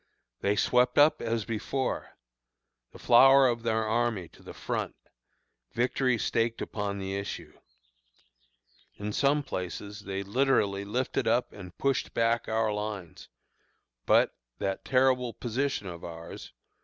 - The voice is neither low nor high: No, low, 115 Hz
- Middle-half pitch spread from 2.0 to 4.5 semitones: Yes, average, 3.9 semitones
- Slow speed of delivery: Yes, slow, 130 wpm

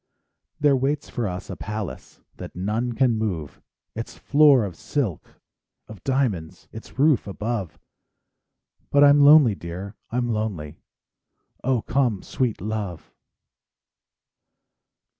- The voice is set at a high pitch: No, low, 110 Hz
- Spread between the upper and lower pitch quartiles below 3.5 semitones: No, average, 5.1 semitones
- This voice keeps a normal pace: No, slow, 115 wpm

